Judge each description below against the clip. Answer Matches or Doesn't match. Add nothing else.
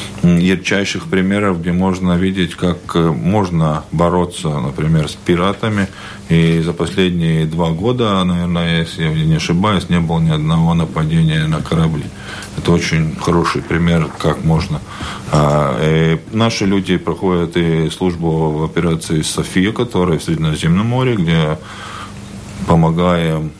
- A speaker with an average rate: Matches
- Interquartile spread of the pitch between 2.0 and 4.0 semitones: Matches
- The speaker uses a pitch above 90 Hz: Doesn't match